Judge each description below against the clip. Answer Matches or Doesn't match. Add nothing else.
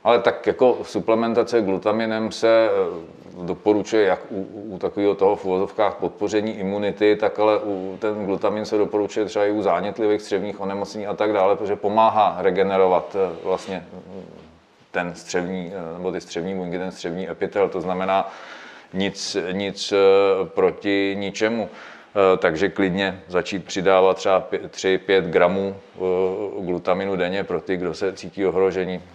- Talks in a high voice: Doesn't match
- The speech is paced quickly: Doesn't match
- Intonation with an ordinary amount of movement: Doesn't match